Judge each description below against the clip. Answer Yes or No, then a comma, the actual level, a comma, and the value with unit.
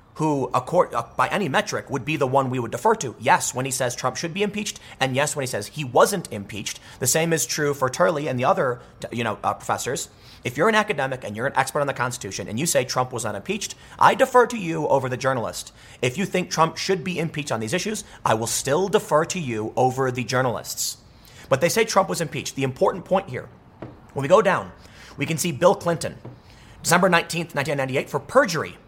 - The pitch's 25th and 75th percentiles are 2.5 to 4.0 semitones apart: No, average, 5.0 semitones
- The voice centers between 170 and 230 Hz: No, medium, 140 Hz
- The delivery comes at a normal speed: No, fast, 220 wpm